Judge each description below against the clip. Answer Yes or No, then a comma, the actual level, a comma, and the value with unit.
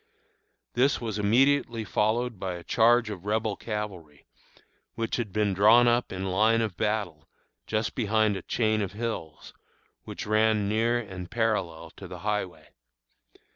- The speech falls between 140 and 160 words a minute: Yes, average, 145 wpm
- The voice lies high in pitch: No, low, 105 Hz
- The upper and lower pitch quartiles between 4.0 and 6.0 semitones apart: No, average, 3.1 semitones